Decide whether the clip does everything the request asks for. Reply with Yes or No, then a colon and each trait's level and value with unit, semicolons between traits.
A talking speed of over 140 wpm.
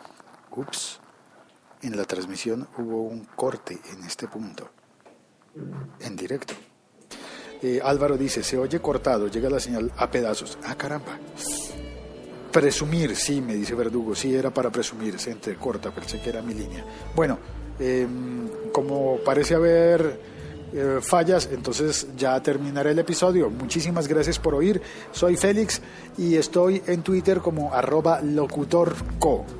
No: average, 130 wpm